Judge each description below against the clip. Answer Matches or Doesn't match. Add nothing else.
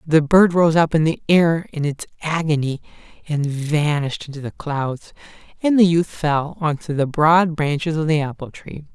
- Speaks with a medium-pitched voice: Matches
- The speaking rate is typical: Matches